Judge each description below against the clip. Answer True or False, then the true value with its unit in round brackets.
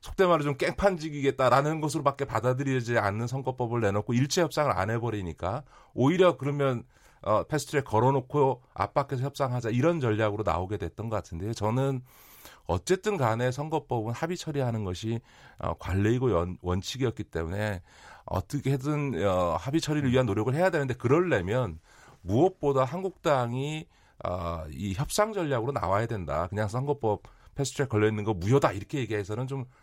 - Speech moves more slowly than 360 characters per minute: False (370 characters per minute)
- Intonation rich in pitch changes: False (5.0 semitones)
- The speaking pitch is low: True (130 Hz)